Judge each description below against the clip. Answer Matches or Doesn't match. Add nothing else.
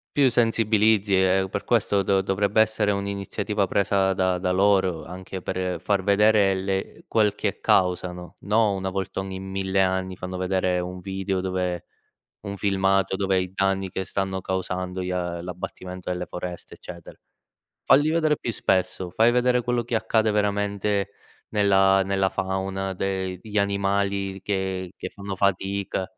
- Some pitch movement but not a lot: Doesn't match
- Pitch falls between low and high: Doesn't match